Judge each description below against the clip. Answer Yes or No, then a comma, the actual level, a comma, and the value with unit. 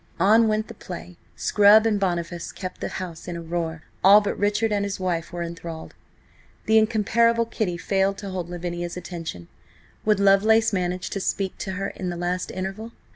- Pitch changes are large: No, average, 3.3 semitones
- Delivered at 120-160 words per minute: No, average, 180 wpm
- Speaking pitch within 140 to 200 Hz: Yes, high, 190 Hz